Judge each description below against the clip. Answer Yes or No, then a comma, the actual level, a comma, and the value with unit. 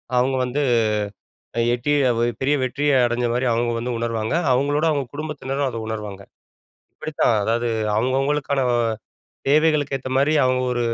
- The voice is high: No, low, 130 Hz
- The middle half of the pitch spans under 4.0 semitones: Yes, average, 3.3 semitones